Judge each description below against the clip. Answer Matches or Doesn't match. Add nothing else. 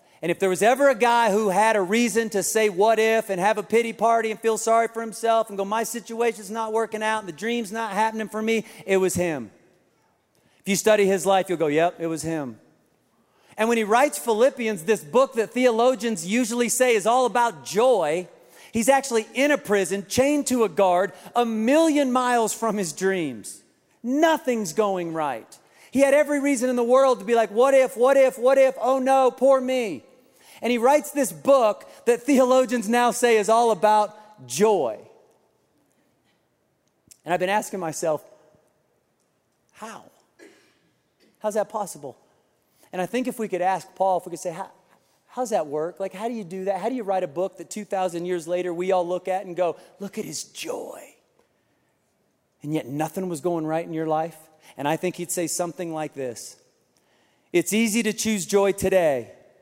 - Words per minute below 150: Doesn't match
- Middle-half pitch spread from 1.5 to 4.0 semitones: Doesn't match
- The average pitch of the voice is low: Doesn't match